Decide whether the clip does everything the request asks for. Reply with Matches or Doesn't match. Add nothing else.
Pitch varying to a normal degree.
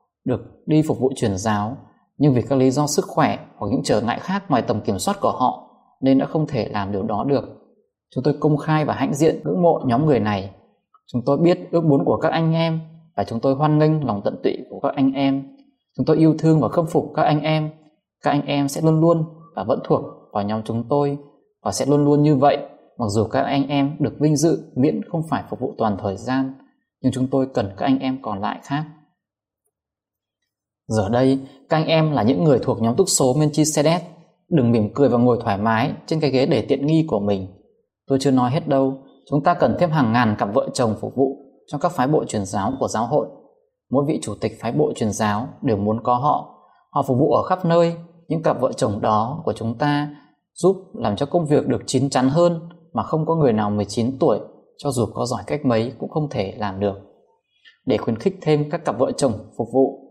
Matches